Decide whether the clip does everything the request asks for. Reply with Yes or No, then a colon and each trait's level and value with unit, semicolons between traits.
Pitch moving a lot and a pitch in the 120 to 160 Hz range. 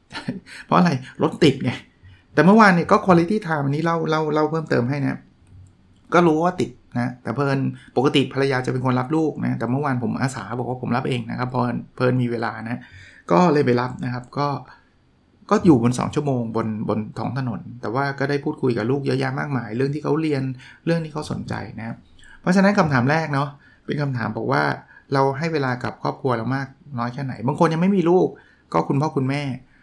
No: average, 3.9 semitones; low, 135 Hz